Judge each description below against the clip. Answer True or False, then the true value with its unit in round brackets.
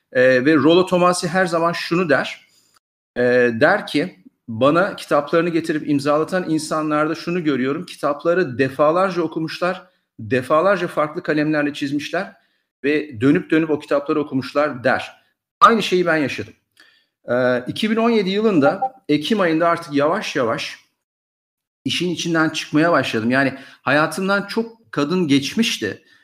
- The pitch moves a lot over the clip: False (3.8 semitones)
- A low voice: False (155 Hz)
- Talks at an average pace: True (120 wpm)